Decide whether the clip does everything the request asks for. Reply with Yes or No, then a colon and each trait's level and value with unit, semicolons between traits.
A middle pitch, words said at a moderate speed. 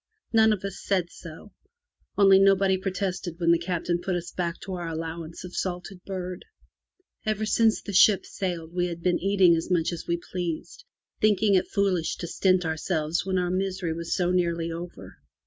Yes: medium, 180 Hz; average, 180 wpm